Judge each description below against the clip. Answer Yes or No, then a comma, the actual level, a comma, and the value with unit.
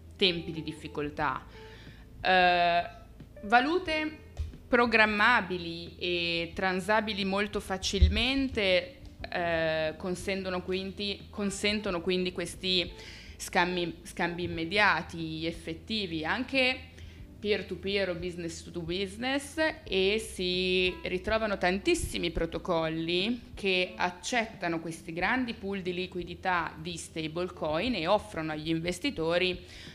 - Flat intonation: No, average, 3.4 semitones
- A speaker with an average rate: No, slow, 85 wpm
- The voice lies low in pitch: No, medium, 180 Hz